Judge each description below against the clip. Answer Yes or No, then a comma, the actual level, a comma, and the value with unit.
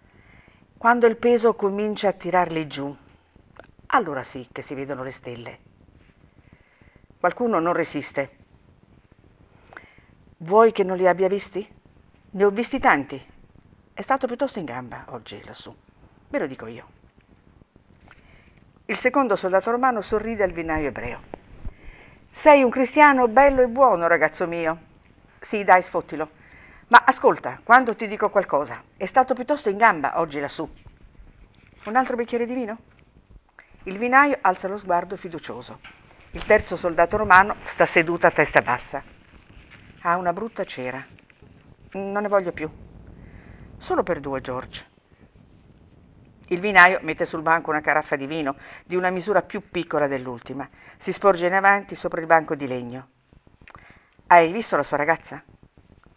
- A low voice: No, medium, 175 Hz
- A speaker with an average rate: Yes, average, 140 wpm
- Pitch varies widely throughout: Yes, wide, 6.7 semitones